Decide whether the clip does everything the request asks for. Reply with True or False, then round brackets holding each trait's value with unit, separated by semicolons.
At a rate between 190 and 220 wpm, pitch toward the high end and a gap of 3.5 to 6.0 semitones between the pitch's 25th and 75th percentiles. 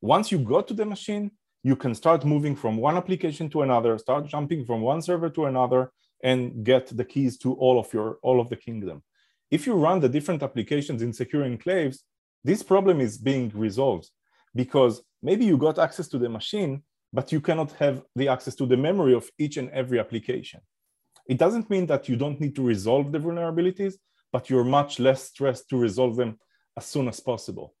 False (200 wpm; 135 Hz; 4.4 semitones)